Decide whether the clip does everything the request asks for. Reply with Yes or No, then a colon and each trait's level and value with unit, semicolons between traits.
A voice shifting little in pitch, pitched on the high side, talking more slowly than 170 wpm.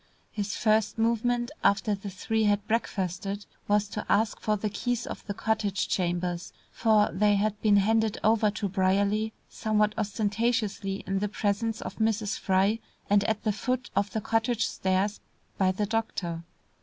Yes: narrow, 1.8 semitones; high, 210 Hz; average, 160 wpm